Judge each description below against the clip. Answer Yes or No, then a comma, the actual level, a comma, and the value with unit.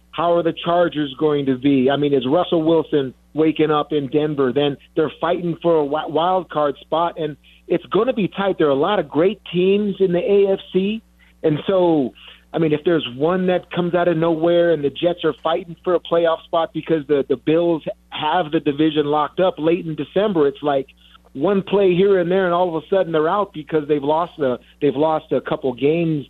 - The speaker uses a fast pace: Yes, fast, 220 wpm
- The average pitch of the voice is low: No, medium, 160 Hz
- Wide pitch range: No, average, 2.8 semitones